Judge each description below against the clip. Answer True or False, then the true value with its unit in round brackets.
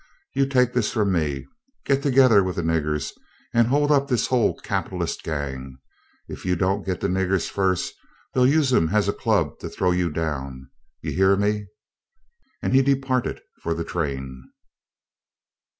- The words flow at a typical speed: True (165 wpm)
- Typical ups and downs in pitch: False (7.5 semitones)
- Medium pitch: False (95 Hz)